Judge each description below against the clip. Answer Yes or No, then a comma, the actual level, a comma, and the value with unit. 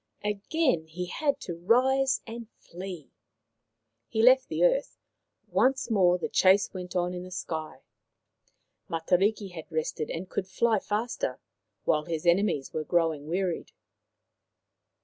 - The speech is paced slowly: Yes, slow, 130 wpm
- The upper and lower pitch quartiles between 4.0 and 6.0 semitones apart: Yes, average, 5.2 semitones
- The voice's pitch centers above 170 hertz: Yes, medium, 185 Hz